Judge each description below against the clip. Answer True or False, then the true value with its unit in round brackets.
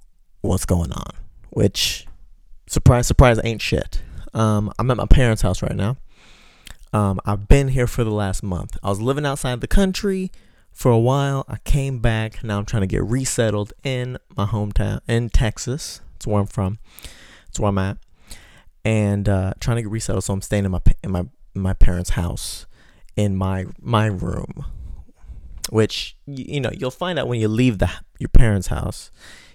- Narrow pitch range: False (4.3 semitones)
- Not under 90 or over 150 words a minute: False (185 wpm)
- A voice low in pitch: True (105 Hz)